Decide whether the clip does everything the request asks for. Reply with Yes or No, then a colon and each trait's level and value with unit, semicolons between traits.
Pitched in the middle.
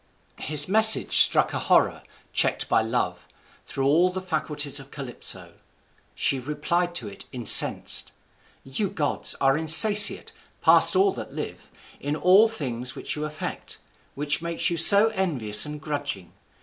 Yes: medium, 150 Hz